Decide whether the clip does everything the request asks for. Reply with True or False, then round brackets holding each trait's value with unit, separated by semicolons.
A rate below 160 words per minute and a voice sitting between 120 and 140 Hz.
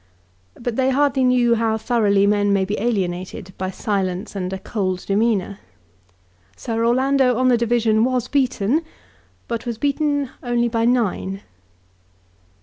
False (140 wpm; 230 Hz)